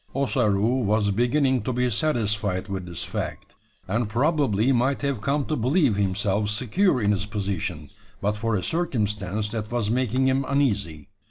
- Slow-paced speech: No, average, 160 wpm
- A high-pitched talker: No, low, 110 Hz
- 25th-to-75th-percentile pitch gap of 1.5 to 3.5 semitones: No, average, 4.4 semitones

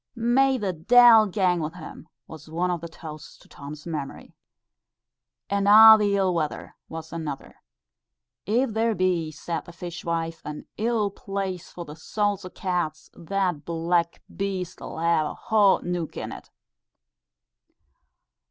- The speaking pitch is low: No, medium, 175 Hz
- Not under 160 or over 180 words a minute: No, average, 145 wpm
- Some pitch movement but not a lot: Yes, average, 3.7 semitones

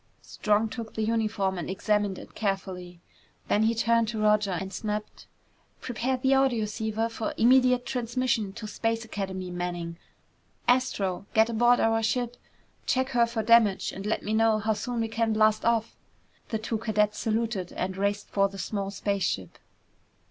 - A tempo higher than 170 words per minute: No, average, 160 wpm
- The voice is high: Yes, high, 220 Hz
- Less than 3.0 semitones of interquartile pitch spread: Yes, narrow, 2.6 semitones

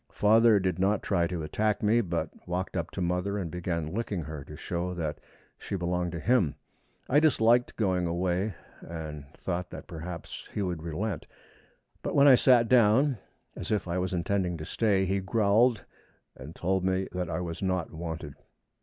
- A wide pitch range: No, average, 3.6 semitones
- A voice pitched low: Yes, very low, 90 Hz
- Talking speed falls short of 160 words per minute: No, average, 180 wpm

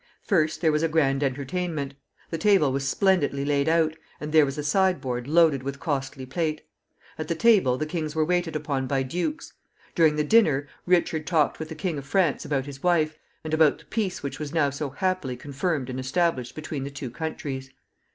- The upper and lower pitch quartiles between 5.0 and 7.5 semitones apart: No, average, 3.4 semitones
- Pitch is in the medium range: Yes, medium, 155 Hz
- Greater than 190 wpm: Yes, average, 200 wpm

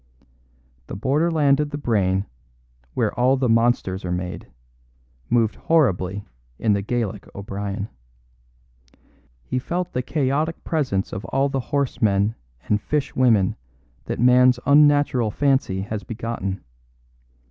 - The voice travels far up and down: Yes, wide, 5.7 semitones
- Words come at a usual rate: No, slow, 125 wpm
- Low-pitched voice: Yes, low, 120 Hz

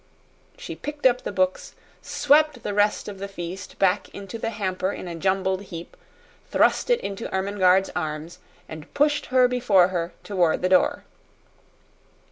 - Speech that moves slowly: No, average, 155 wpm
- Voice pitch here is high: Yes, high, 195 Hz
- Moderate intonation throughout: Yes, average, 3.8 semitones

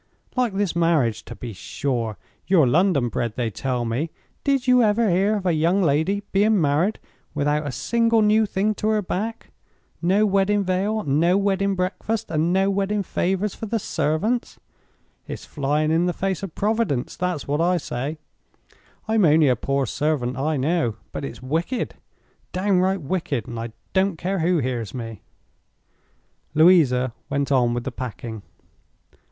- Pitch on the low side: No, medium, 170 Hz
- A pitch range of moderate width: No, wide, 6.4 semitones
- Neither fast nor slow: Yes, average, 160 wpm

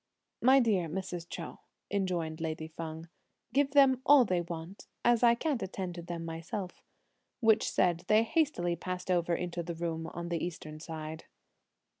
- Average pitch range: Yes, average, 4.7 semitones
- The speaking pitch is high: No, medium, 175 Hz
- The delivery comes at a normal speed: Yes, average, 160 wpm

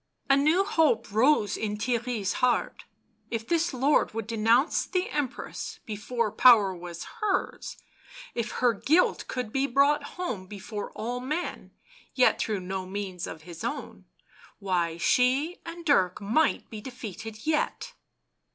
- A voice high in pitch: Yes, high, 235 Hz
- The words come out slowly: No, average, 145 wpm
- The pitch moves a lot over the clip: Yes, wide, 5.8 semitones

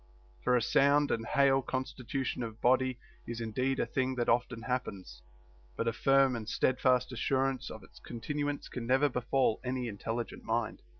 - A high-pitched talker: No, low, 125 Hz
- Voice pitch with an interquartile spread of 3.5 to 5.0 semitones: No, narrow, 2.5 semitones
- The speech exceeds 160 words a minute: Yes, average, 170 wpm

